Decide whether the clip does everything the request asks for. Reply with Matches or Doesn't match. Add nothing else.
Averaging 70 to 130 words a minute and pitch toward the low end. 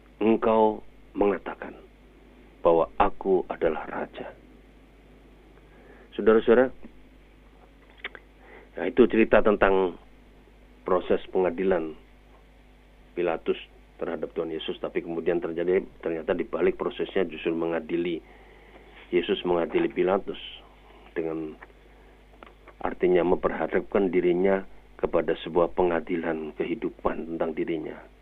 Matches